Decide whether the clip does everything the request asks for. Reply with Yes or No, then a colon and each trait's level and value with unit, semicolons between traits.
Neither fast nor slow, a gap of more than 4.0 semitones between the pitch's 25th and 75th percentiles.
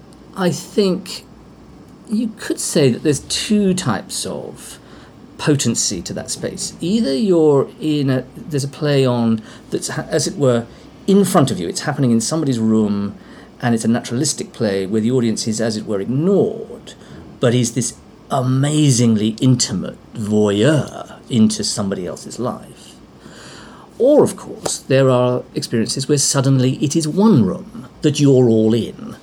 Yes: average, 150 wpm; average, 5.3 semitones